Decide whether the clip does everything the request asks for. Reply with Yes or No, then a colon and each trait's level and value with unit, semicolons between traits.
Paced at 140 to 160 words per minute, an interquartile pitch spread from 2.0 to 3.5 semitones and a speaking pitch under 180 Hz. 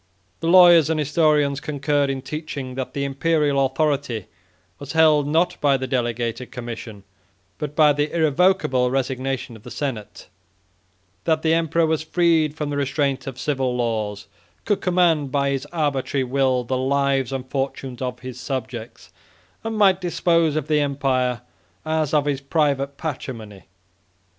Yes: average, 150 wpm; average, 3.2 semitones; medium, 140 Hz